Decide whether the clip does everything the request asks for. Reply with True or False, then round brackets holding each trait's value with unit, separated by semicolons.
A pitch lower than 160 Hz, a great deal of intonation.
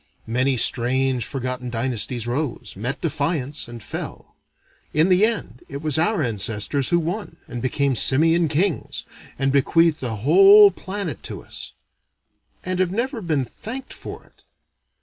True (140 Hz; 5.8 semitones)